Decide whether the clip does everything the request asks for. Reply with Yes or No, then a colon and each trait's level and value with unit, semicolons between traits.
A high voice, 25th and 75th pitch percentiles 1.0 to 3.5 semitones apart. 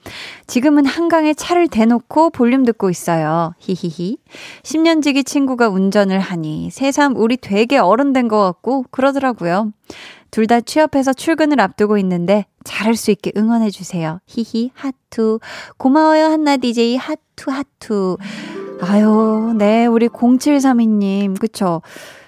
No: high, 230 Hz; average, 5.3 semitones